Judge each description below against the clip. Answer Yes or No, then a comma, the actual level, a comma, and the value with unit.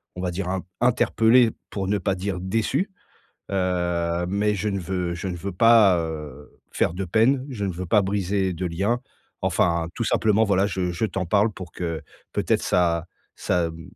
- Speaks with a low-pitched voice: Yes, very low, 95 Hz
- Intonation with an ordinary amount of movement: Yes, average, 3.0 semitones